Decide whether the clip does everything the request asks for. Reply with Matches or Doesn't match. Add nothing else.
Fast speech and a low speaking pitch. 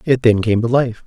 Matches